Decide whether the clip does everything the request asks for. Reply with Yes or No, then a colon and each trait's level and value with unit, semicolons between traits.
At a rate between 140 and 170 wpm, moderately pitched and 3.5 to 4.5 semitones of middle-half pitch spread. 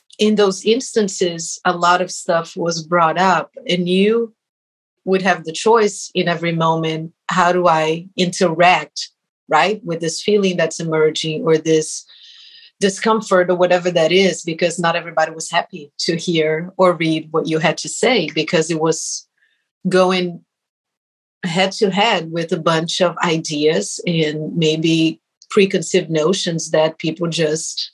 No: average, 150 wpm; medium, 170 Hz; average, 2.8 semitones